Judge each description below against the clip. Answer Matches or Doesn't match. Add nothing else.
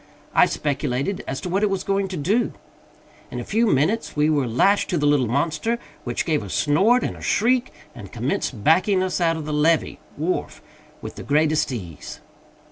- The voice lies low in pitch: Doesn't match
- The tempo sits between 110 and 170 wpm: Doesn't match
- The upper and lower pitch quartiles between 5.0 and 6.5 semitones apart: Matches